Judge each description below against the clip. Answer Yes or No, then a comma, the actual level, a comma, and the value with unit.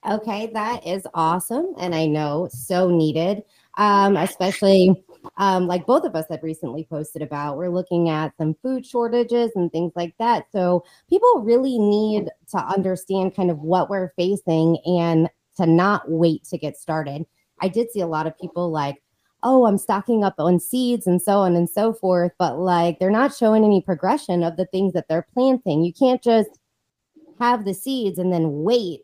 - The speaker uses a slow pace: No, average, 185 wpm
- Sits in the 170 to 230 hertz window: Yes, medium, 185 Hz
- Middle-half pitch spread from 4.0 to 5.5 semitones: Yes, average, 4.3 semitones